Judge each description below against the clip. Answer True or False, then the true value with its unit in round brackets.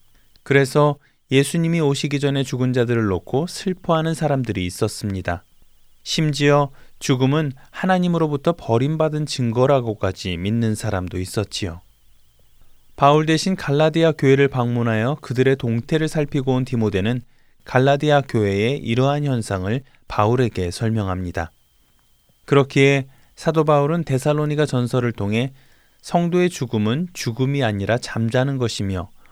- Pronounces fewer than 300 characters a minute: False (310 characters per minute)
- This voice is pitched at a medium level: False (130 Hz)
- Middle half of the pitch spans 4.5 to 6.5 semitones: True (5.1 semitones)